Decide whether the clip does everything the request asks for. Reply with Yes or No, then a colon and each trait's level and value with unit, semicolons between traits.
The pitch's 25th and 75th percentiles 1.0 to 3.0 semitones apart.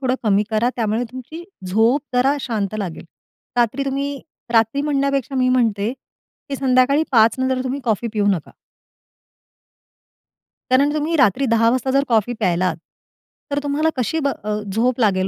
No: average, 4.1 semitones